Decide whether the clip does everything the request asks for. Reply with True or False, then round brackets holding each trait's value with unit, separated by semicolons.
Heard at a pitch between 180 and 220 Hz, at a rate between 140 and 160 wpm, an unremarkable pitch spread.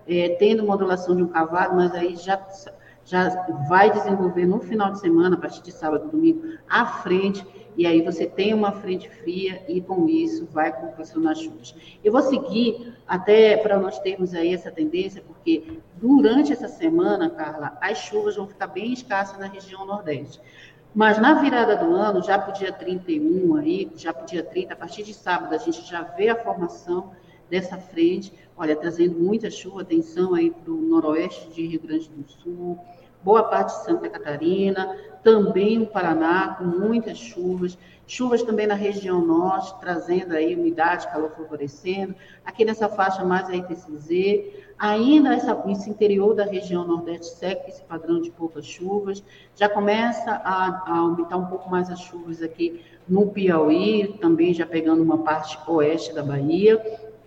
False (185 Hz; 170 wpm; 3.9 semitones)